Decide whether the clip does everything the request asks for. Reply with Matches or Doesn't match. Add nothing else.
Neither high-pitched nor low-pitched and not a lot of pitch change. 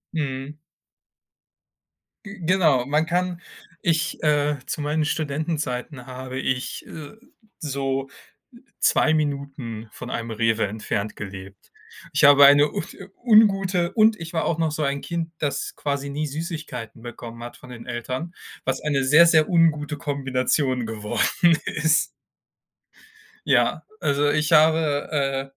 Doesn't match